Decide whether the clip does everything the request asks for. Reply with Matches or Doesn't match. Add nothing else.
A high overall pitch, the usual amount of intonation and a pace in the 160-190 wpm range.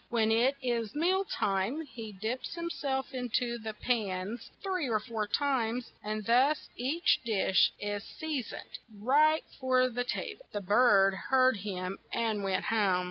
Matches